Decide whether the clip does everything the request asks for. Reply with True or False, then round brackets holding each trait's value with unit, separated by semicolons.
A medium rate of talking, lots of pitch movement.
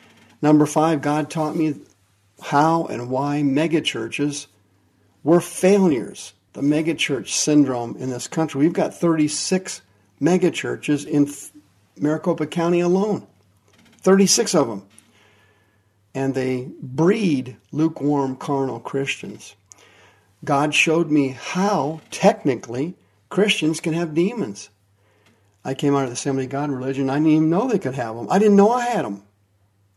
False (130 wpm; 6.7 semitones)